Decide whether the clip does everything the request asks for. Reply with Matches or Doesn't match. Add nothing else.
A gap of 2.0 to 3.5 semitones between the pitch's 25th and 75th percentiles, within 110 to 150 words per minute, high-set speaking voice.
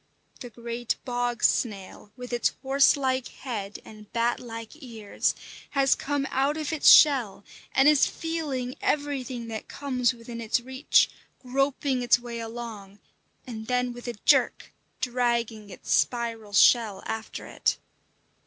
Matches